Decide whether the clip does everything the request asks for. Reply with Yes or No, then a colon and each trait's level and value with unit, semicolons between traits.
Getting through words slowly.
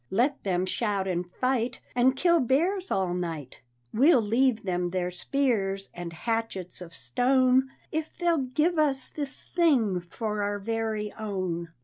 No: average, 145 wpm